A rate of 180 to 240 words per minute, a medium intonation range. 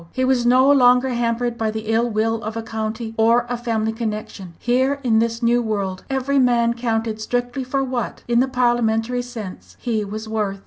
No: average, 190 wpm; narrow, 2.0 semitones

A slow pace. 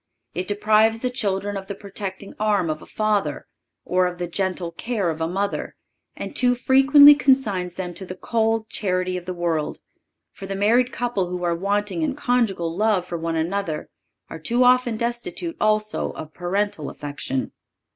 No: average, 175 wpm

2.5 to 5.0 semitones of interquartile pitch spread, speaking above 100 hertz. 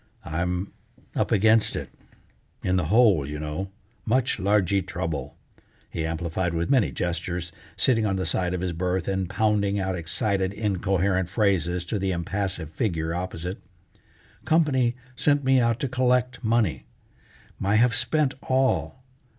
No: average, 4.4 semitones; very low, 95 Hz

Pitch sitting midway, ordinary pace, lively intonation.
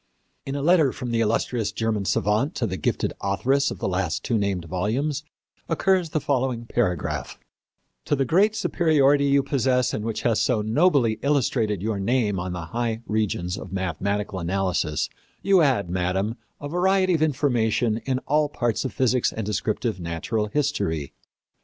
No: low, 115 Hz; average, 165 wpm; wide, 5.9 semitones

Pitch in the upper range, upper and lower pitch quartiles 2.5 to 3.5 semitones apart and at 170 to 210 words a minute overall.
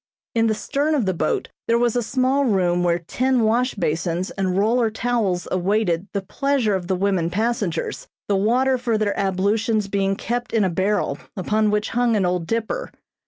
No: high, 210 Hz; average, 4.1 semitones; average, 185 wpm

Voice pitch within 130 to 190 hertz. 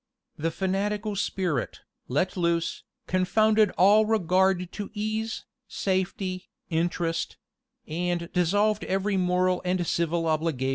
Yes: medium, 185 Hz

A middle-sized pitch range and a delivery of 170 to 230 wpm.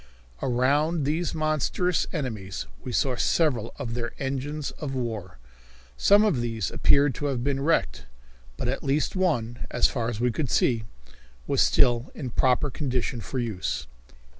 No: average, 3.8 semitones; average, 160 wpm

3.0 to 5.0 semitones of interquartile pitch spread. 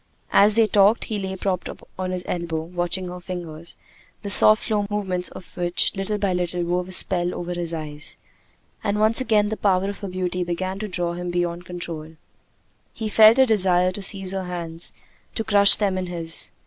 No: narrow, 2.6 semitones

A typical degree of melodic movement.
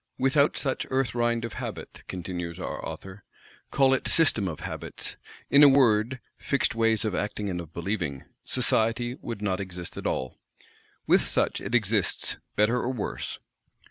Yes: average, 4.8 semitones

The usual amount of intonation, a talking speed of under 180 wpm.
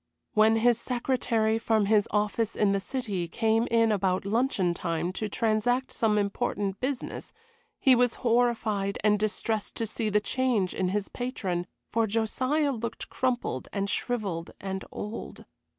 Yes: average, 3.1 semitones; average, 150 wpm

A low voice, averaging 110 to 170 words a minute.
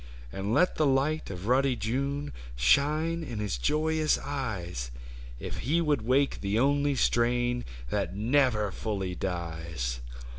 Yes: low, 120 Hz; slow, 135 wpm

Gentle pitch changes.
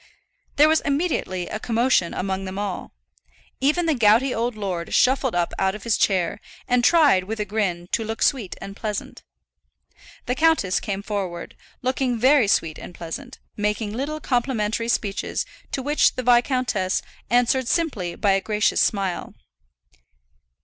No: average, 4.9 semitones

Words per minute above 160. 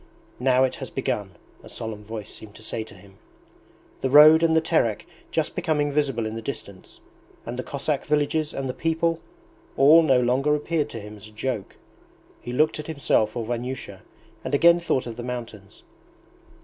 Yes: average, 185 wpm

